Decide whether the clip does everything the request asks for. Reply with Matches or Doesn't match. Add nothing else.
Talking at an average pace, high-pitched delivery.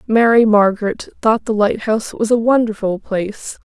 Matches